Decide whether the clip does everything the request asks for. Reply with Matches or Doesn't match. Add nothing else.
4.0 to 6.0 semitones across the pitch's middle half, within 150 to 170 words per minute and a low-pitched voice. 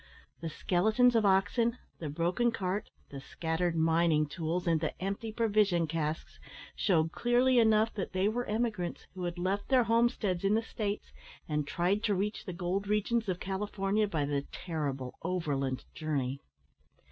Doesn't match